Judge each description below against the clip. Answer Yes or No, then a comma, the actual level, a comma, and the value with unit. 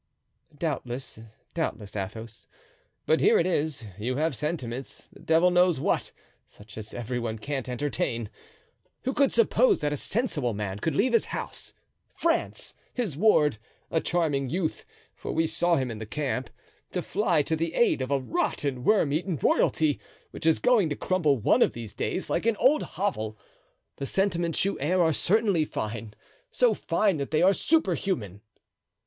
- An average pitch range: No, wide, 6.7 semitones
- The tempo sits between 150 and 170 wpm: Yes, average, 165 wpm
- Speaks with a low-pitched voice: No, medium, 150 Hz